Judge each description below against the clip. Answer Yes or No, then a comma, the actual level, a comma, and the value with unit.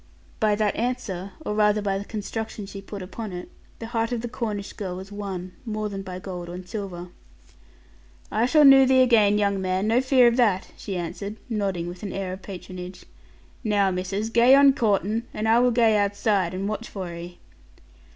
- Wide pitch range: No, average, 3.3 semitones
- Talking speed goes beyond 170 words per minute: Yes, average, 195 wpm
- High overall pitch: Yes, high, 205 Hz